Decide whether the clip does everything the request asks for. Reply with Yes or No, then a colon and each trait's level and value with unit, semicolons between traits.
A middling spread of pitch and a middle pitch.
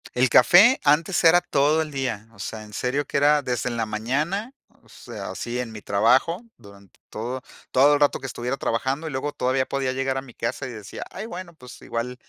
No: average, 3.8 semitones; low, 130 Hz